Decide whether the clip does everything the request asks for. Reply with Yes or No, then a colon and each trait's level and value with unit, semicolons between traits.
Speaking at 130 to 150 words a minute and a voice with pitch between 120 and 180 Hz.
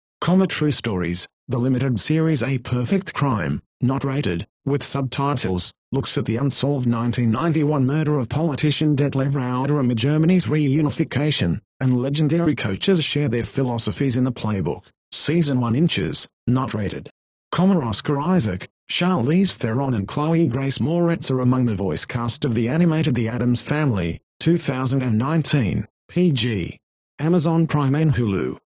Yes: average, 140 wpm; low, 135 Hz